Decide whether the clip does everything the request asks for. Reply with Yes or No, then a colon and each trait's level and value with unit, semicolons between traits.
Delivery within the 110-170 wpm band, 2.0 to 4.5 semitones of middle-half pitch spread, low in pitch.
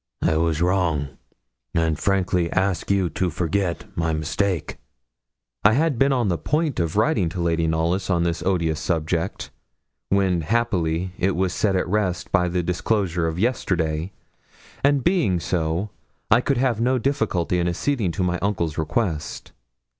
Yes: average, 155 wpm; average, 3.9 semitones; very low, 90 Hz